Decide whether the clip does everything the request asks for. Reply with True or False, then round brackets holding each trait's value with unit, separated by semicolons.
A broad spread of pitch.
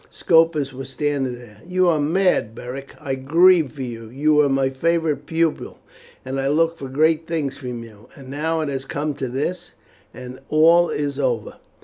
False (3.6 semitones)